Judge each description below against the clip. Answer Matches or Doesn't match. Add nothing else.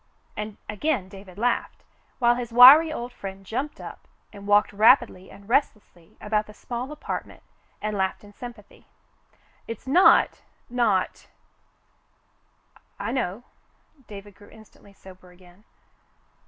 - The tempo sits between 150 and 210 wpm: Doesn't match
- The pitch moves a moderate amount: Matches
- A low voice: Doesn't match